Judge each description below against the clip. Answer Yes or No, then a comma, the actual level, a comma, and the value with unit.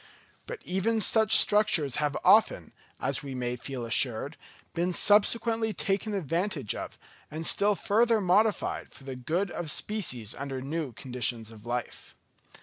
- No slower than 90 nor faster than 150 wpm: Yes, average, 145 wpm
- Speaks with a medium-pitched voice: Yes, medium, 165 Hz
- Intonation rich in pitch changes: Yes, wide, 8.2 semitones